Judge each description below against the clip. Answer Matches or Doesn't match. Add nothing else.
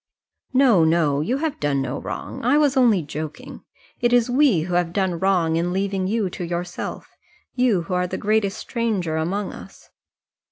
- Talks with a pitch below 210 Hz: Matches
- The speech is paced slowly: Doesn't match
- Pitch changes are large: Matches